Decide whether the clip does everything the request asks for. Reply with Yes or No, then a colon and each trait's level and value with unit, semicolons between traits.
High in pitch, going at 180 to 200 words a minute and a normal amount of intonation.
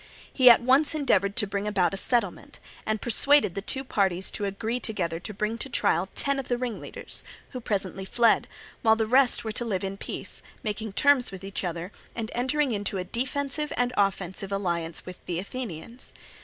Yes: high, 215 Hz; average, 190 wpm; average, 4.4 semitones